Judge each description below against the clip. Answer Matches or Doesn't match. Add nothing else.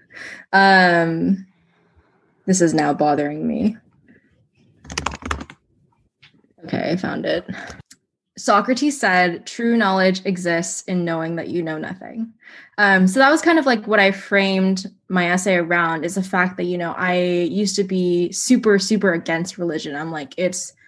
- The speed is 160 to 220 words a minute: Doesn't match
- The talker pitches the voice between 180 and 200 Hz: Matches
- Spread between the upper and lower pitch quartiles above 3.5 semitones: Doesn't match